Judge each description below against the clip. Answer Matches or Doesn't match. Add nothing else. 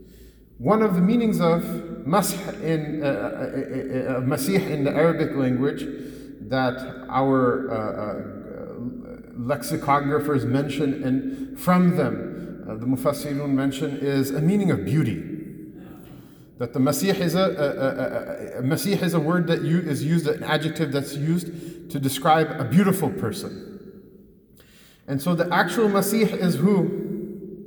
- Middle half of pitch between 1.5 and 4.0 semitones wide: Doesn't match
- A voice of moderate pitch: Matches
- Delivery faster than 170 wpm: Doesn't match